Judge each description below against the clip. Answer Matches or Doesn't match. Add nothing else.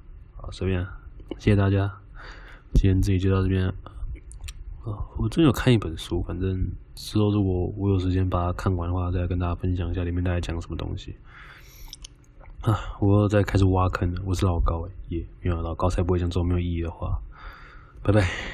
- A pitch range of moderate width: Doesn't match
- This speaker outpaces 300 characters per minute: Matches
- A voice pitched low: Matches